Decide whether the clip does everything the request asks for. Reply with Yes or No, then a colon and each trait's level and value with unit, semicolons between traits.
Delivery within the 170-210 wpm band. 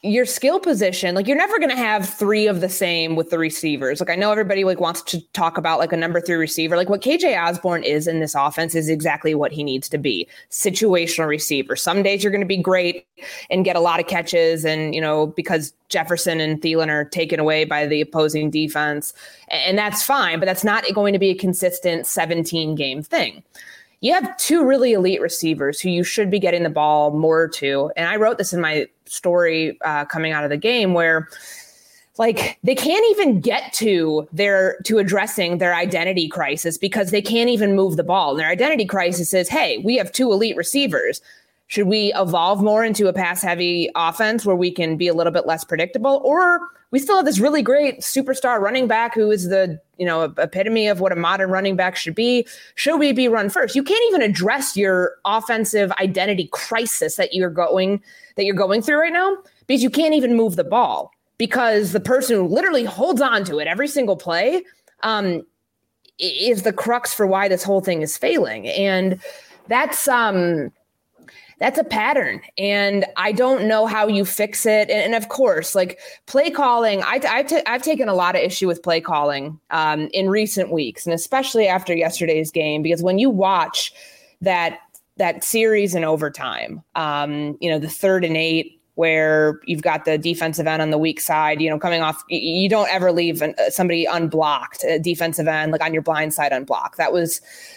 Yes: average, 200 wpm